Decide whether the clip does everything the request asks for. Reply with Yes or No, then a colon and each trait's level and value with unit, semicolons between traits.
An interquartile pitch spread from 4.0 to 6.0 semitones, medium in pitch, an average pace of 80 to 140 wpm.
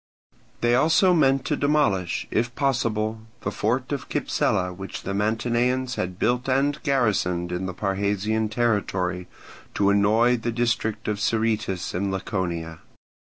No: average, 4.3 semitones; low, 110 Hz; slow, 135 wpm